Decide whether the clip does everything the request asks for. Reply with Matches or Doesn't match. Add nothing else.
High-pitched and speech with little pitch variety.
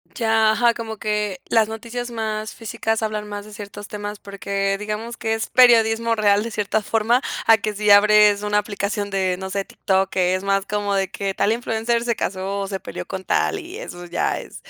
Matches